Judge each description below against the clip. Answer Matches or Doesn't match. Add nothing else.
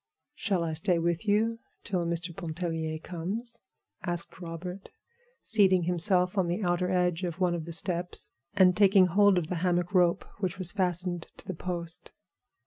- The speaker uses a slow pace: Doesn't match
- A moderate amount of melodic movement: Doesn't match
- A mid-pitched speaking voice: Matches